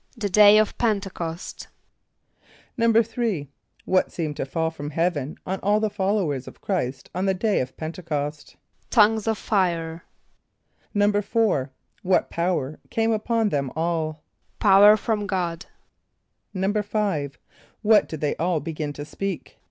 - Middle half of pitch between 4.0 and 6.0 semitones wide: Yes, average, 4.9 semitones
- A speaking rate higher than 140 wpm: No, slow, 135 wpm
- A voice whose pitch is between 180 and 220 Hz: Yes, medium, 185 Hz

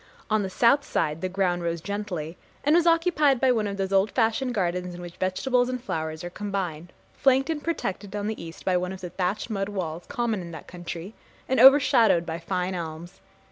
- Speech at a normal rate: No, fast, 210 wpm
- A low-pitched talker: No, high, 195 Hz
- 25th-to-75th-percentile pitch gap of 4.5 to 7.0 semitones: Yes, wide, 5.5 semitones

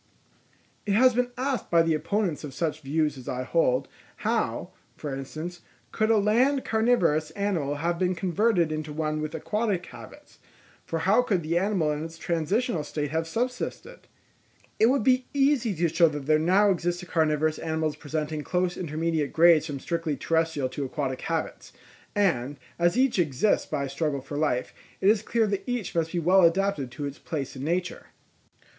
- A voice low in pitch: No, medium, 165 Hz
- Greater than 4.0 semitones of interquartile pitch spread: Yes, average, 4.7 semitones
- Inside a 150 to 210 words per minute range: Yes, average, 175 wpm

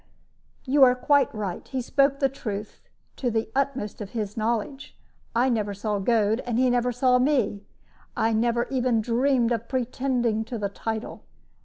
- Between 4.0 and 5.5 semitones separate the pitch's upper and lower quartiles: No, average, 3.0 semitones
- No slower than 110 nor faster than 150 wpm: No, average, 165 wpm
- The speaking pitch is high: Yes, high, 235 Hz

